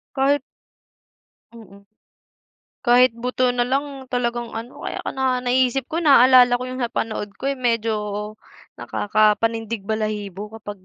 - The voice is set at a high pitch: Yes, high, 240 Hz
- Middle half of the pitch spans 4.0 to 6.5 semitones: No, average, 2.7 semitones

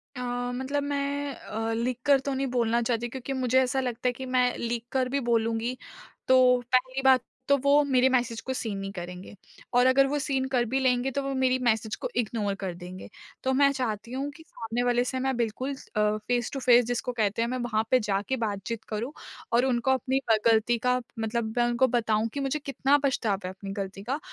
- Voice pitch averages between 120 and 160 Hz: No, high, 245 Hz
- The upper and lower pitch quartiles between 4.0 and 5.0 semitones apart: No, average, 2.8 semitones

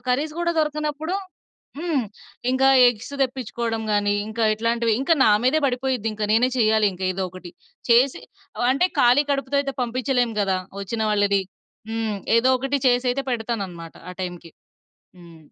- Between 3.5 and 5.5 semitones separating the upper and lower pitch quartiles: Yes, average, 4.3 semitones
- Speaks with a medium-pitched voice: No, high, 235 Hz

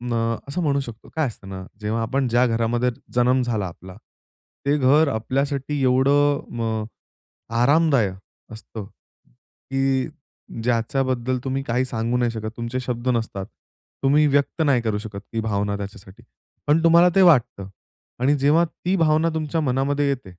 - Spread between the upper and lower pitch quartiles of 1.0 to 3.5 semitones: No, average, 3.9 semitones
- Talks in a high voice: No, low, 125 Hz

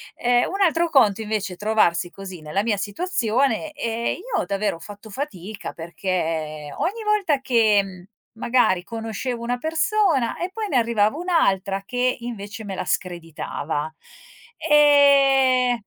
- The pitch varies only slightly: No, wide, 6.2 semitones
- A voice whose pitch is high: Yes, high, 230 Hz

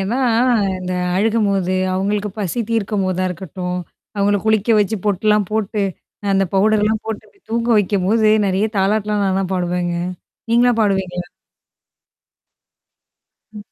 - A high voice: Yes, high, 200 Hz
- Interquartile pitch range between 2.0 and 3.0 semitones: Yes, narrow, 2.5 semitones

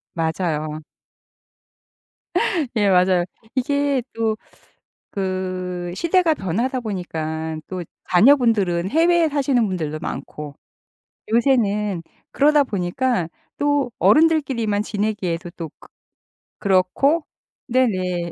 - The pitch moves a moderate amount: No, wide, 6.9 semitones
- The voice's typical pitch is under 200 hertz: No, high, 205 Hz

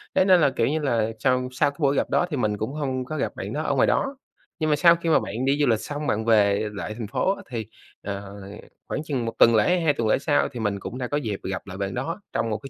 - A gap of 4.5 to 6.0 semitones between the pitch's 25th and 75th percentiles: Yes, wide, 5.5 semitones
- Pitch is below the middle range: Yes, low, 125 Hz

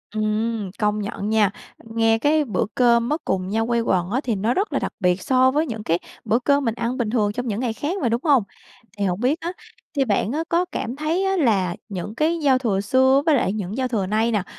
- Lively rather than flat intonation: No, average, 4.1 semitones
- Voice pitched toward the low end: No, high, 230 Hz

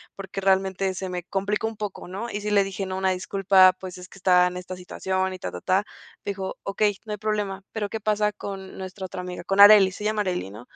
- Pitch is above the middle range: Yes, high, 195 Hz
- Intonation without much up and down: Yes, narrow, 1.7 semitones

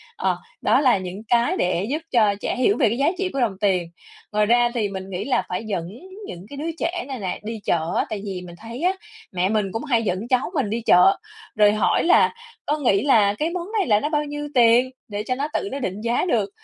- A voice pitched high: Yes, high, 230 Hz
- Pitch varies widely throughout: Yes, wide, 5.8 semitones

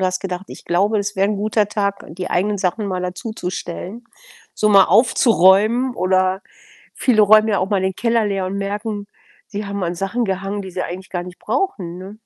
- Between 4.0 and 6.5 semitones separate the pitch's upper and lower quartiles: No, narrow, 2.4 semitones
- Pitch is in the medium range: No, high, 200 Hz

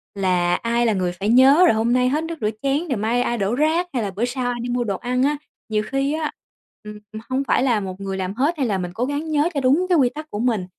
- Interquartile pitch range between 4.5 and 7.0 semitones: Yes, average, 5.2 semitones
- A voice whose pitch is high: Yes, high, 245 Hz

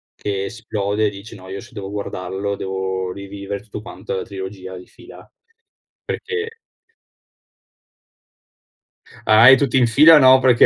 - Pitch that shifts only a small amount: No, average, 4.0 semitones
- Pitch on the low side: Yes, low, 100 Hz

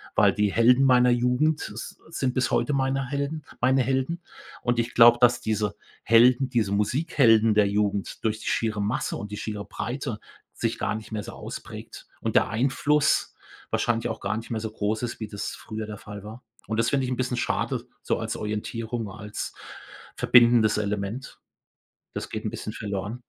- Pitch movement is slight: No, average, 3.1 semitones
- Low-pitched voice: Yes, low, 115 Hz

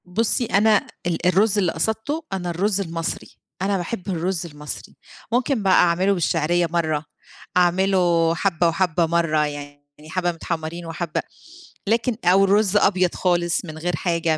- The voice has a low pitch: No, medium, 175 Hz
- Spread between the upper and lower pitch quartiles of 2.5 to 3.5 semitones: Yes, average, 2.9 semitones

